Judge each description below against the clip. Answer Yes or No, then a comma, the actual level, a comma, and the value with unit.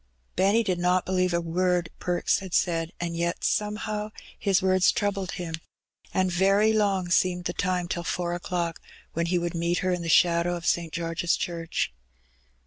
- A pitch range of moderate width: No, narrow, 1.6 semitones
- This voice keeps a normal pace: Yes, average, 175 wpm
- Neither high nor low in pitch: Yes, medium, 180 Hz